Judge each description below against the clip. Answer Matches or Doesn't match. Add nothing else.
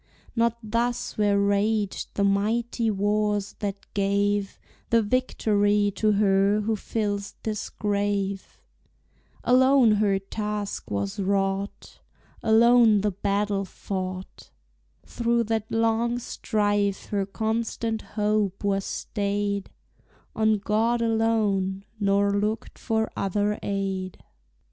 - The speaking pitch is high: Matches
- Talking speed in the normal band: Doesn't match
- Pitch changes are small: Matches